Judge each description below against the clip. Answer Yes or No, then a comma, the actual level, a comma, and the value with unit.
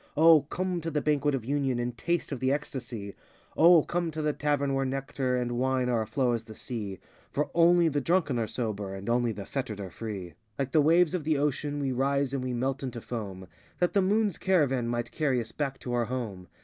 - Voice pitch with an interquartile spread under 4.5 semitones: Yes, average, 4.1 semitones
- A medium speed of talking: No, fast, 230 wpm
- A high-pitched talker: No, low, 135 Hz